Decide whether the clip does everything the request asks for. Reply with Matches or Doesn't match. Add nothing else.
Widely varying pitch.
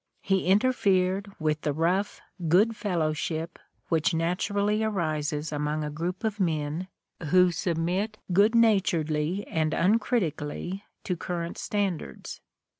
Doesn't match